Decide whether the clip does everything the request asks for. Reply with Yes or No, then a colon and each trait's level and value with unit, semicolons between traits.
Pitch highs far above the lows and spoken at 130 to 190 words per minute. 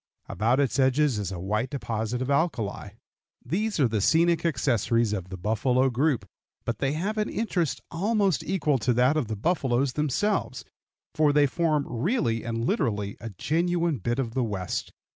Yes: wide, 6.1 semitones; average, 170 wpm